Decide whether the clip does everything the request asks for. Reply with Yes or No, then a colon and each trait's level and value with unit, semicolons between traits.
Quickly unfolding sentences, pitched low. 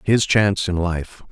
No: average, 180 wpm; very low, 95 Hz